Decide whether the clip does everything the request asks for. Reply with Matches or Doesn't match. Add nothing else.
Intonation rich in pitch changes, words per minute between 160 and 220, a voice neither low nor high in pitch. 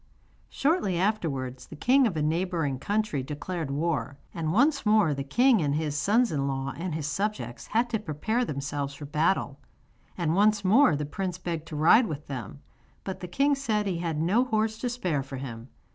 Matches